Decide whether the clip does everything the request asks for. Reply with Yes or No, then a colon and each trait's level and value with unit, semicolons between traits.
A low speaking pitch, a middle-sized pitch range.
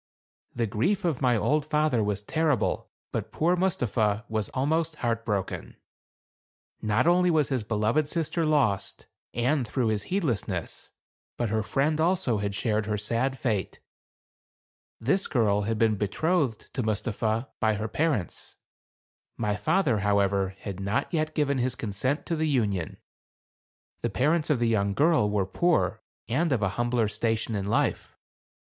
No: low, 115 Hz; wide, 6.5 semitones